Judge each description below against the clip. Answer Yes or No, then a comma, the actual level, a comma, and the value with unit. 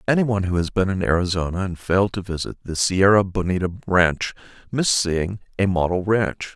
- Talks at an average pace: Yes, average, 185 wpm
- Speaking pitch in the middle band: No, very low, 95 Hz